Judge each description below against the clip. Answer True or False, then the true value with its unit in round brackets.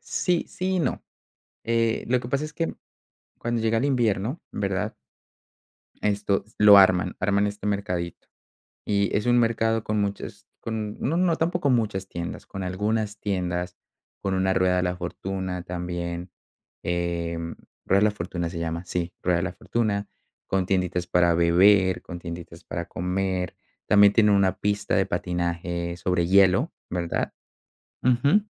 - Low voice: True (95 Hz)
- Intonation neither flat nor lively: True (3.6 semitones)